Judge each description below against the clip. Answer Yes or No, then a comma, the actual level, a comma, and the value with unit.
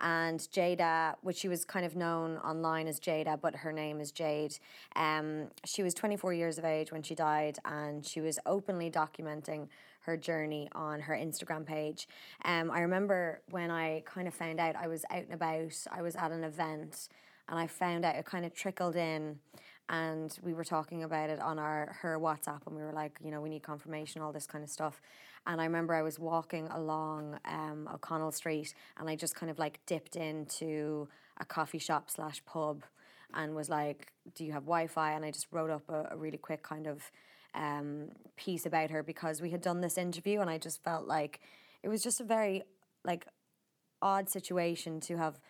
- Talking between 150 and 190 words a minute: No, fast, 205 wpm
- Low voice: No, medium, 160 Hz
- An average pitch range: No, narrow, 1.7 semitones